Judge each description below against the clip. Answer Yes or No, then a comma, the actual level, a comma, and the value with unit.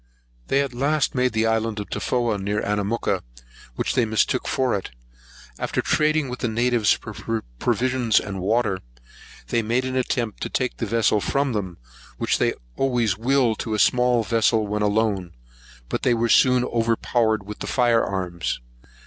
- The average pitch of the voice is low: Yes, low, 115 Hz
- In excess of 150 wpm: Yes, average, 170 wpm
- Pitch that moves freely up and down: No, average, 3.0 semitones